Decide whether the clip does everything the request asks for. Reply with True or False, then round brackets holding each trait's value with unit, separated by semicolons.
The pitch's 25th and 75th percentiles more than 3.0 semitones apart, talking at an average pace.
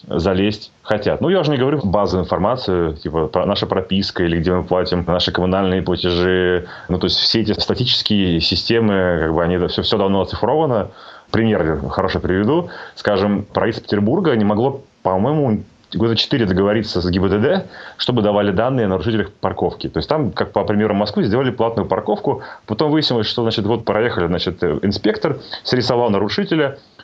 False (3.6 semitones; 165 wpm)